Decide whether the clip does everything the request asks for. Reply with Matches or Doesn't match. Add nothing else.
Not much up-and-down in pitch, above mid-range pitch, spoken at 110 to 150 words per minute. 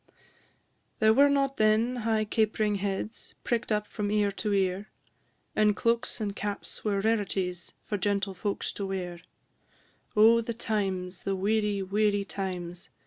Matches